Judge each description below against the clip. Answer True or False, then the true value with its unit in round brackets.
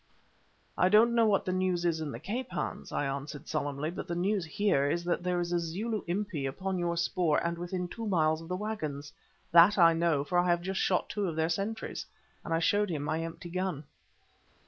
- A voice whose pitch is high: False (175 Hz)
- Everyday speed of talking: False (220 wpm)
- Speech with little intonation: False (3.1 semitones)